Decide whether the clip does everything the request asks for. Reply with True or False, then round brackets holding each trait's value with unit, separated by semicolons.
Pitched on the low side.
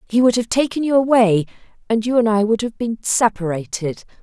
False (225 Hz)